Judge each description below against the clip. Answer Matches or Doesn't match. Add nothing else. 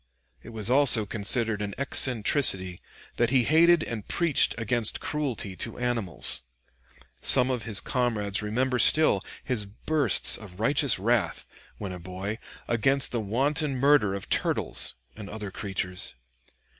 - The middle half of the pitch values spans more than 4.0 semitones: Matches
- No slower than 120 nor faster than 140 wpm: Matches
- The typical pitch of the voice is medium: Doesn't match